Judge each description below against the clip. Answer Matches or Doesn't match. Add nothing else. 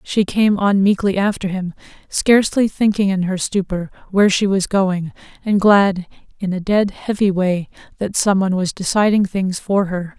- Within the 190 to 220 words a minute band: Doesn't match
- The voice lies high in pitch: Matches